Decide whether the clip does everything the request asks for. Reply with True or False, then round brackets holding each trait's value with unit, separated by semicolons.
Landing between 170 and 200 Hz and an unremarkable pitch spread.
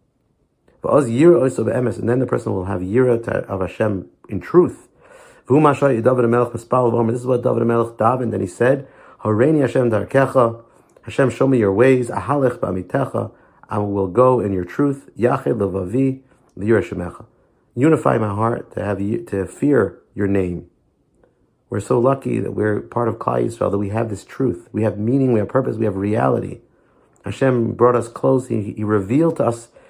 False (115 Hz; 4.0 semitones)